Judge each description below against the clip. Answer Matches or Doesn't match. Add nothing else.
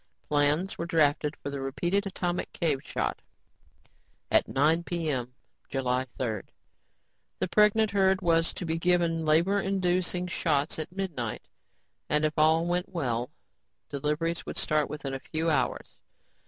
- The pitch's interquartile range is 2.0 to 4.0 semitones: Matches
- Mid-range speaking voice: Matches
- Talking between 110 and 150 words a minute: Matches